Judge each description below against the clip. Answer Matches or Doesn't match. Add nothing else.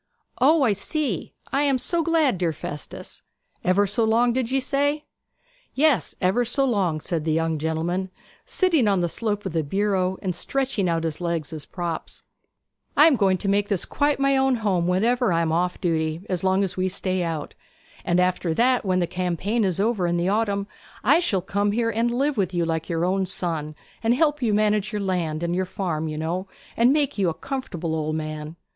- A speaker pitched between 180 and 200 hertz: Matches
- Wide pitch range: Matches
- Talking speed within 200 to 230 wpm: Matches